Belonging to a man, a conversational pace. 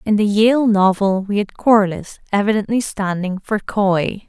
No: female; average, 155 wpm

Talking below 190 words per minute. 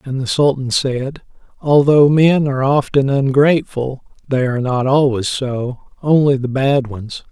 Yes: average, 150 wpm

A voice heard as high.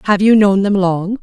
Yes: high, 200 Hz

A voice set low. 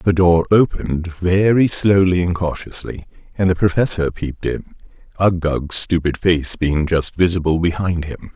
Yes: very low, 85 Hz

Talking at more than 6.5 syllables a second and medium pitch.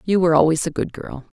Yes: 6.8 syllables/s; medium, 165 Hz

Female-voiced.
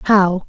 Yes: female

